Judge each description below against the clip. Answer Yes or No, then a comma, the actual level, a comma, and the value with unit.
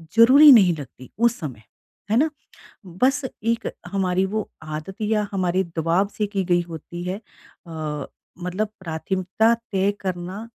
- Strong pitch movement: No, average, 4.0 semitones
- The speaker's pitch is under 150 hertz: No, high, 190 Hz